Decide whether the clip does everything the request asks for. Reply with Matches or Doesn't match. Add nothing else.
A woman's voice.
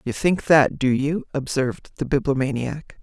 Matches